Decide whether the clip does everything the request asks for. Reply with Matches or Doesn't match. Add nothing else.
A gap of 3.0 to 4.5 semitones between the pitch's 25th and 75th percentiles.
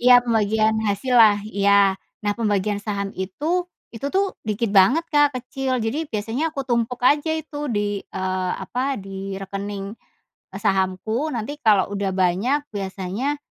Doesn't match